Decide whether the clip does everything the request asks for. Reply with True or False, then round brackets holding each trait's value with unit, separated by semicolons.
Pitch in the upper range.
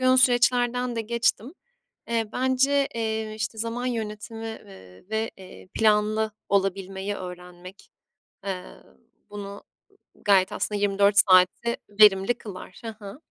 True (215 Hz)